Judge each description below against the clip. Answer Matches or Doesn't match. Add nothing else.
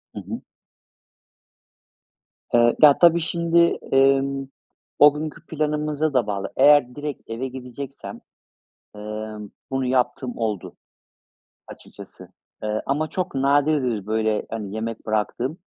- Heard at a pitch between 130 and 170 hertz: Matches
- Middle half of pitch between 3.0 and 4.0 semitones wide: Doesn't match